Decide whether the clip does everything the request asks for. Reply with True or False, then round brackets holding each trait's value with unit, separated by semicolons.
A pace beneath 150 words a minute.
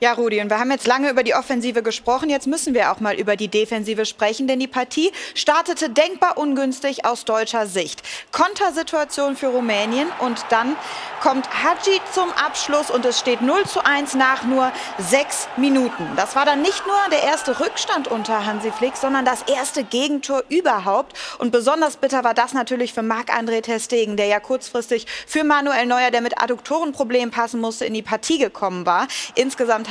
False (180 wpm)